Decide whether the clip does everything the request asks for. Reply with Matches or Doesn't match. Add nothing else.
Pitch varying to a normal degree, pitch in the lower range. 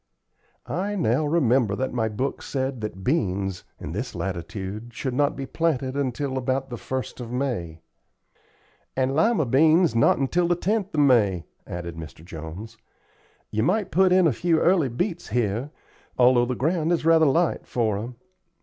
Doesn't match